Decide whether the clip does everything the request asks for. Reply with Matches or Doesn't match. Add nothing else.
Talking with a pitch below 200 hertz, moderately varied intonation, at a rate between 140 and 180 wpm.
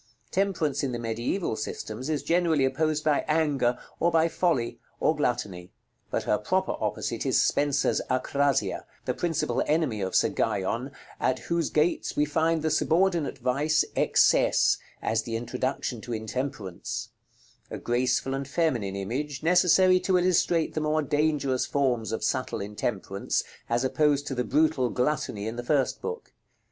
Matches